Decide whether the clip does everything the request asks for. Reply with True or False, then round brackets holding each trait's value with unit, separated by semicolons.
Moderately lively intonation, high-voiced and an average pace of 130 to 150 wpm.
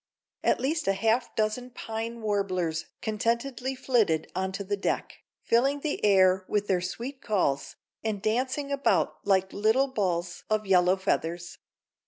True (4.4 semitones; 210 Hz; 140 wpm)